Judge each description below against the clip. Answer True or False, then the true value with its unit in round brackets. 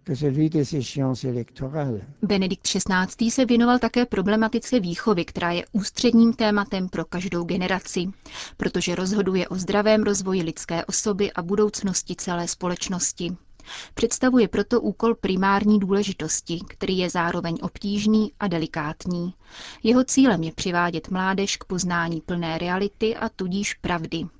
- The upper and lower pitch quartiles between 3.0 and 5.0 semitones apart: True (3.5 semitones)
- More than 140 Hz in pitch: True (190 Hz)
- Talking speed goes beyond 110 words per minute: True (120 wpm)